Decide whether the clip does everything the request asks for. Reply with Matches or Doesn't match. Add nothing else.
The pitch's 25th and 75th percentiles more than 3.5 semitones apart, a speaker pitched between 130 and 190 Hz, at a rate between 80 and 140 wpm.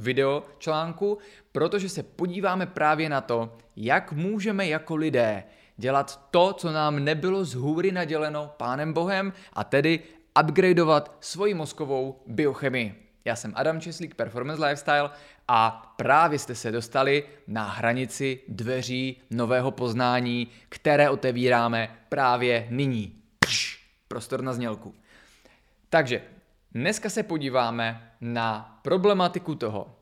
Matches